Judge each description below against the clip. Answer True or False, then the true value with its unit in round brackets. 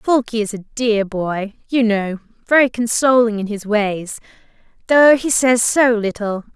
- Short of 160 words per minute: True (145 wpm)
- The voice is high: True (225 Hz)